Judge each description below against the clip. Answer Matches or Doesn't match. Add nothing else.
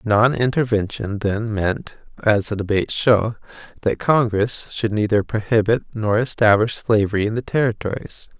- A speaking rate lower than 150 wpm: Matches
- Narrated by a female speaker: Doesn't match